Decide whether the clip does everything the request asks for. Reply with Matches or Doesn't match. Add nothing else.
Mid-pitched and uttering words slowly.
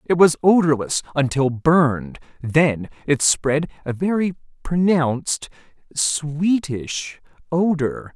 Matches